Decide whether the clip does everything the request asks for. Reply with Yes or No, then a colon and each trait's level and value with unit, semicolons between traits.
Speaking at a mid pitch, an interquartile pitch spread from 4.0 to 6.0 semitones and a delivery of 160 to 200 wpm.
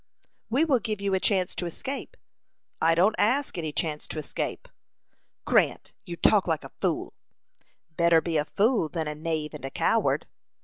Yes: medium, 170 Hz; average, 5.2 semitones; average, 175 wpm